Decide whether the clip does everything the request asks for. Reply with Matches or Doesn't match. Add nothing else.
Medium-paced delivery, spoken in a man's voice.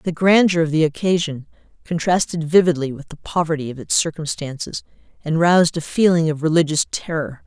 Doesn't match